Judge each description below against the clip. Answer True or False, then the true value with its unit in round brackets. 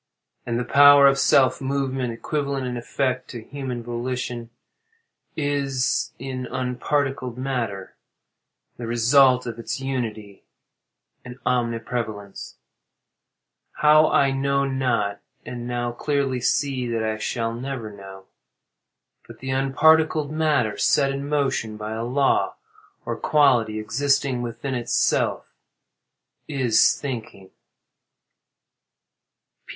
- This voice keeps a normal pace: False (110 wpm)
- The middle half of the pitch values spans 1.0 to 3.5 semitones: True (2.9 semitones)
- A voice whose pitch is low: True (125 Hz)